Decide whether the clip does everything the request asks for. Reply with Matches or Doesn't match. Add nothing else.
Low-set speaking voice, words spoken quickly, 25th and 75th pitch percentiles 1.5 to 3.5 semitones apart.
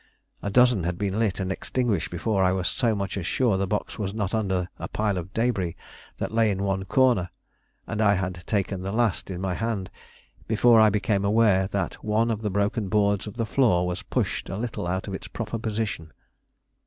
Matches